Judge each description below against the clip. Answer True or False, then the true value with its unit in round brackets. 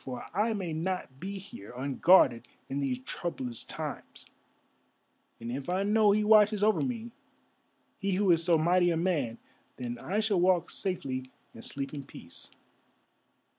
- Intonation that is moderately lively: False (7.1 semitones)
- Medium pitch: True (175 Hz)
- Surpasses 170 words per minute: False (155 wpm)